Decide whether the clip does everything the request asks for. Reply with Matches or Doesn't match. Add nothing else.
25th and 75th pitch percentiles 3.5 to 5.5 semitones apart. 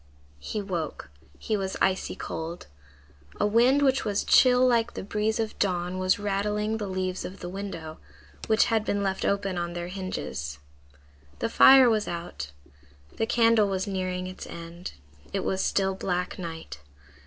Doesn't match